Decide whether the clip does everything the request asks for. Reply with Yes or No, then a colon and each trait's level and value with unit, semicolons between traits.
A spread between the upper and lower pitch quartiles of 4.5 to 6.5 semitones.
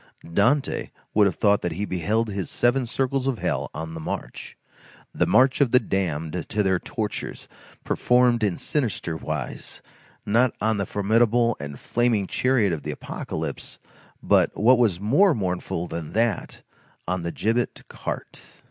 Yes: average, 5.1 semitones